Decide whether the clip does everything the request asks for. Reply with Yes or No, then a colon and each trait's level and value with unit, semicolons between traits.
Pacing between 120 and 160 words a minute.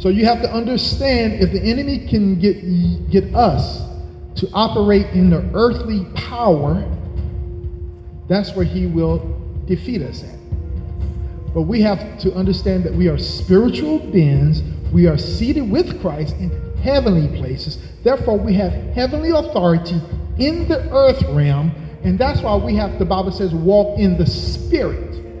Yes: average, 150 wpm